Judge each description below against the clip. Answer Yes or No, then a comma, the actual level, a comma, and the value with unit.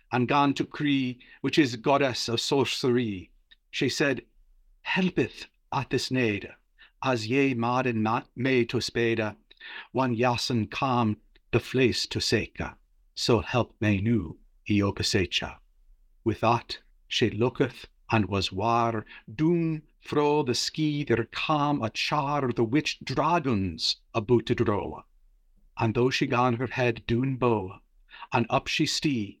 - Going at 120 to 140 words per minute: Yes, slow, 135 wpm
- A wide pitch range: No, average, 3.3 semitones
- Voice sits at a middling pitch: No, low, 120 Hz